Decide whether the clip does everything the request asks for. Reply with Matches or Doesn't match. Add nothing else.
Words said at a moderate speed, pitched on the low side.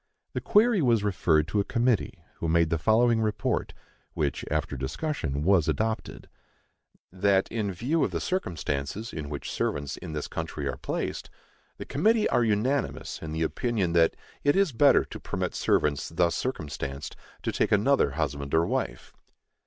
Matches